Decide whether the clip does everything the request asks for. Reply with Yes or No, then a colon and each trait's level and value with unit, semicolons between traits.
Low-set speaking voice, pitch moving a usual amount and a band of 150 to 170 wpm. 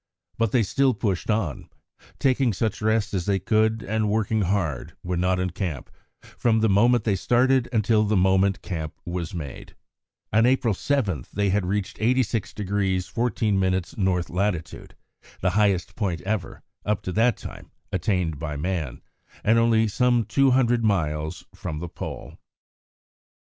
Yes: low, 100 Hz; average, 3.6 semitones; average, 155 wpm